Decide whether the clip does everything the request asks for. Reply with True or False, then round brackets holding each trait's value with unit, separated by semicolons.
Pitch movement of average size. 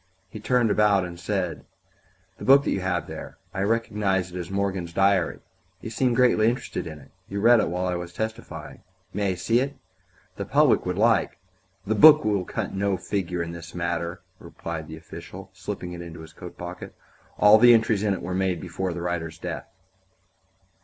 True (3.5 semitones)